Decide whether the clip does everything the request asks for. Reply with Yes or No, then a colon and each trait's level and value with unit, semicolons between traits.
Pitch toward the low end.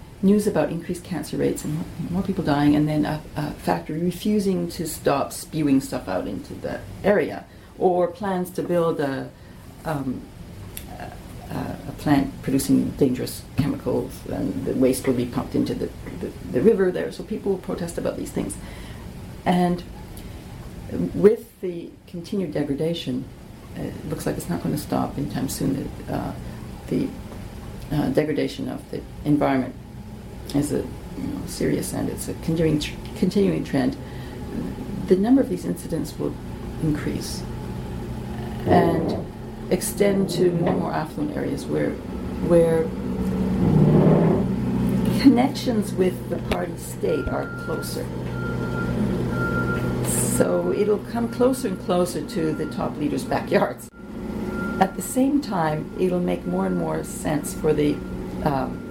No: medium, 155 Hz